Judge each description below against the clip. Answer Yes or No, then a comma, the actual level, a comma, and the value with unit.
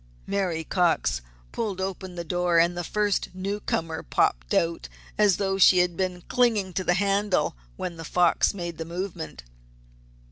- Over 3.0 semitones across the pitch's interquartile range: No, narrow, 2.6 semitones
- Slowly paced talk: No, average, 155 wpm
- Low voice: No, medium, 180 Hz